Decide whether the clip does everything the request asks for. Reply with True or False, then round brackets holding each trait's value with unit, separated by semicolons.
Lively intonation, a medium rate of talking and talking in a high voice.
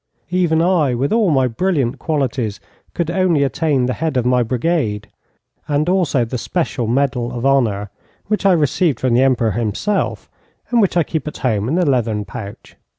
False (5.8 semitones; 180 wpm; 135 Hz)